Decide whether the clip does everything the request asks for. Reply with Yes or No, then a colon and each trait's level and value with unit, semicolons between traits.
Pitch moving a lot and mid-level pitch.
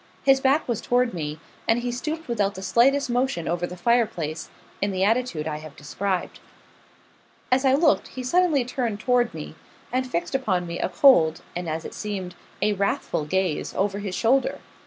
No: wide, 6.4 semitones; high, 210 Hz